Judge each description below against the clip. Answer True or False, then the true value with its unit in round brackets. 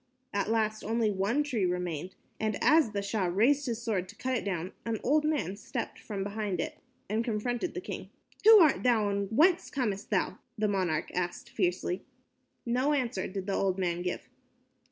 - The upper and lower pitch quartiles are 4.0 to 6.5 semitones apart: True (4.4 semitones)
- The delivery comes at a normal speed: True (185 wpm)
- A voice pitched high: True (215 Hz)